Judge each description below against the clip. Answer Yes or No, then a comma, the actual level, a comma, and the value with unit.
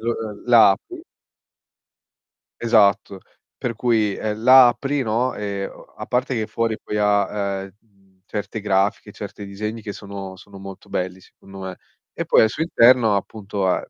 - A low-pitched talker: Yes, low, 105 Hz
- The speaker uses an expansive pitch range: No, average, 2.8 semitones